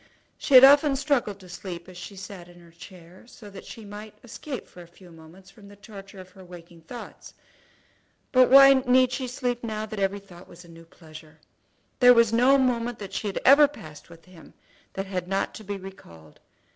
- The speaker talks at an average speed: No, fast, 210 wpm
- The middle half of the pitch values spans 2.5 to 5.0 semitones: No, wide, 5.6 semitones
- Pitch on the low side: No, high, 200 Hz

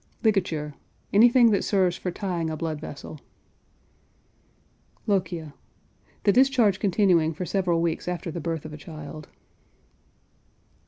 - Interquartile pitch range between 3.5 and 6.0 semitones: Yes, average, 3.9 semitones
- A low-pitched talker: No, medium, 175 Hz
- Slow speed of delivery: Yes, slow, 120 wpm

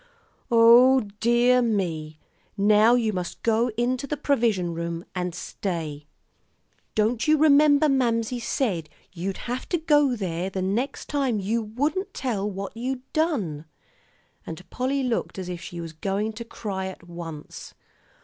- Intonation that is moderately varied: No, wide, 5.8 semitones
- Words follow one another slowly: No, average, 145 wpm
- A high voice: Yes, high, 220 Hz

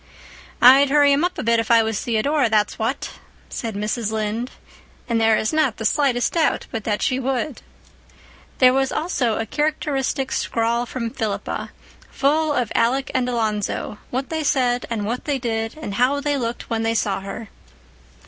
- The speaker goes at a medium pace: Yes, average, 175 wpm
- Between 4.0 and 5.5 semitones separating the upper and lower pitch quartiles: No, average, 3.5 semitones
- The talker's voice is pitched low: No, high, 240 Hz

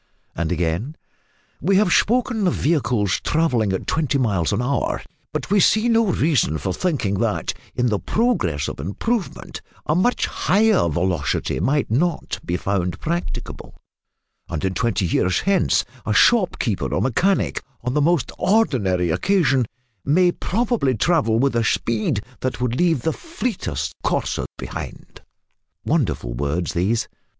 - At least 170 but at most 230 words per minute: No, average, 140 wpm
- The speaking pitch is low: Yes, low, 125 Hz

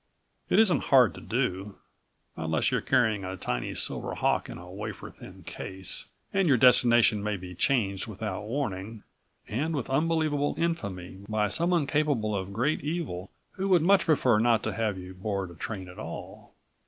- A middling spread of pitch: No, wide, 7.2 semitones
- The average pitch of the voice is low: Yes, low, 110 Hz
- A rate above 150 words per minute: Yes, average, 170 wpm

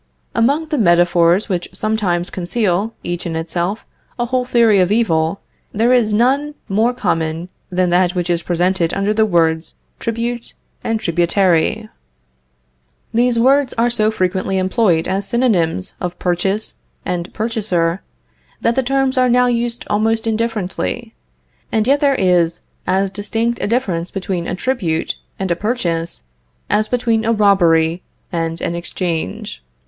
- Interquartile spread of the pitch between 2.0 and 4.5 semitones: No, average, 5.0 semitones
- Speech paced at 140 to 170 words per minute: Yes, average, 145 wpm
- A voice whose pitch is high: Yes, high, 200 Hz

